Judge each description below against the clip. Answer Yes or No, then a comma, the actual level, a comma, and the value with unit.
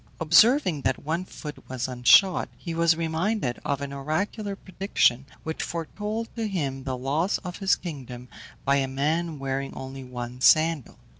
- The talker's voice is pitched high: No, medium, 155 Hz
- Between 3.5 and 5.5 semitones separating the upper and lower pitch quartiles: Yes, average, 5.1 semitones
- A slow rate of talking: No, average, 155 wpm